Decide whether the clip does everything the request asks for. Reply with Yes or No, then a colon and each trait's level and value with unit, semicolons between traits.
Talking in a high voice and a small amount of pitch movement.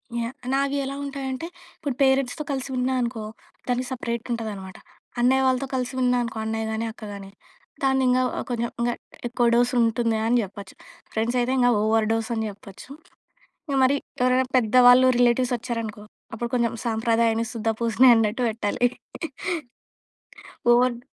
Yes: high, 240 Hz; narrow, 2.2 semitones